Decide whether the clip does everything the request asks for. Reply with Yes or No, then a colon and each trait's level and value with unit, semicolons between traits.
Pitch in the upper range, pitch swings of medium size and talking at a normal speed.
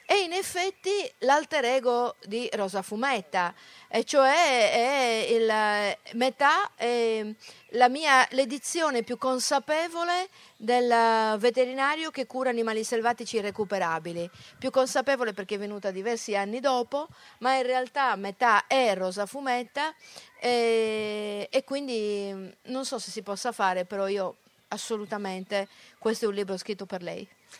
Yes: high, 235 Hz; average, 4.4 semitones; average, 130 wpm